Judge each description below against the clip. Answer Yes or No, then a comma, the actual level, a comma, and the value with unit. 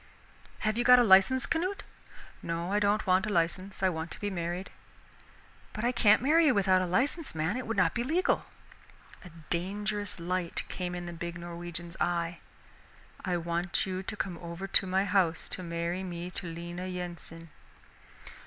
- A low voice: No, medium, 185 Hz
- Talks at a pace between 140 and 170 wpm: No, average, 180 wpm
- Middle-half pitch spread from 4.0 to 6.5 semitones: No, average, 3.1 semitones